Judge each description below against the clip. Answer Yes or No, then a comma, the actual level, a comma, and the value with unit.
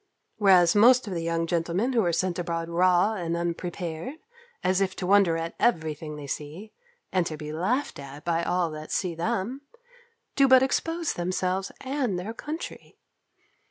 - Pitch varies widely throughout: No, average, 4.2 semitones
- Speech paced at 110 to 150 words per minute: No, average, 170 wpm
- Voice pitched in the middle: Yes, medium, 180 Hz